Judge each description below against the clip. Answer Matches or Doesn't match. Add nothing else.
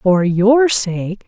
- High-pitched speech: Matches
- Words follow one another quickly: Doesn't match